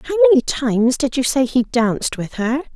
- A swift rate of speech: Yes, fast, 220 wpm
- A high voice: Yes, very high, 265 Hz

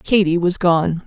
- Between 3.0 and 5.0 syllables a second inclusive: Yes, 3.9 syllables/s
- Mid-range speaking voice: Yes, medium, 180 Hz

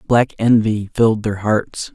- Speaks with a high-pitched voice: No, low, 110 Hz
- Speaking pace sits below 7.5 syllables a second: Yes, 4.0 syllables/s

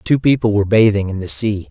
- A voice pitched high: No, low, 105 Hz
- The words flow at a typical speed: No, fast, 245 wpm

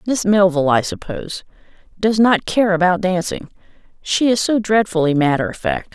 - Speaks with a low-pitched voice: No, high, 190 Hz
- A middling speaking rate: Yes, average, 160 wpm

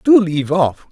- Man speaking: Yes, male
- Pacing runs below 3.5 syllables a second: No, 5.0 syllables/s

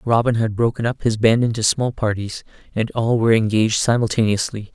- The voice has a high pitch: No, low, 115 Hz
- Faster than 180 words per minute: No, average, 175 wpm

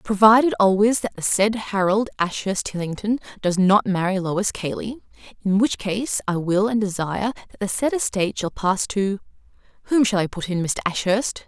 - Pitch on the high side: Yes, high, 205 Hz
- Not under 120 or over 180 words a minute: Yes, average, 175 wpm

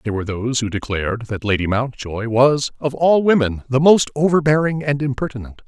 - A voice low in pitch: Yes, low, 130 Hz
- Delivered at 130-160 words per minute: No, average, 180 wpm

